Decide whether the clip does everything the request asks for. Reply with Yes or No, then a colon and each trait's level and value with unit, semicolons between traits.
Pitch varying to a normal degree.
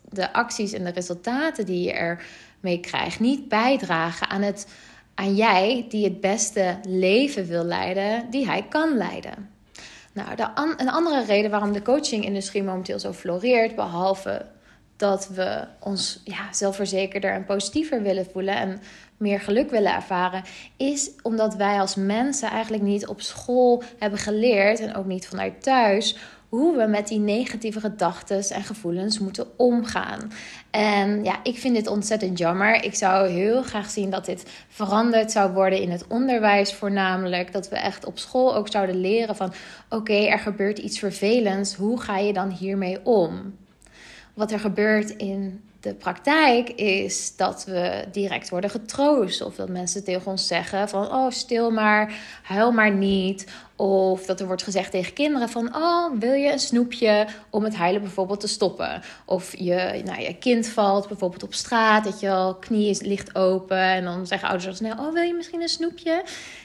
Yes: average, 3.0 semitones